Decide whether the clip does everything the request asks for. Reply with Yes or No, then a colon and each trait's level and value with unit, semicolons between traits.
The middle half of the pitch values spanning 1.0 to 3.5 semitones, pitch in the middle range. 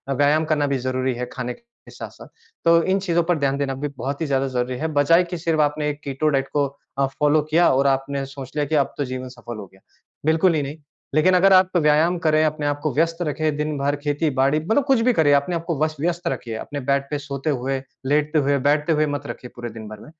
Yes: average, 2.8 semitones; medium, 145 Hz